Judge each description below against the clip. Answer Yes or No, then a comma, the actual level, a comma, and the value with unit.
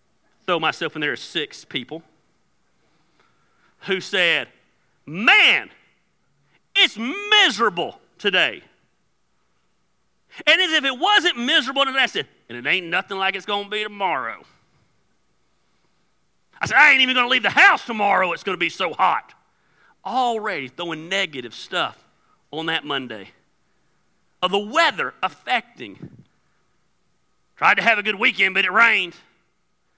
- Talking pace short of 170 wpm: Yes, average, 140 wpm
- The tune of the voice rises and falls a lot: Yes, wide, 7.9 semitones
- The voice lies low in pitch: No, high, 195 Hz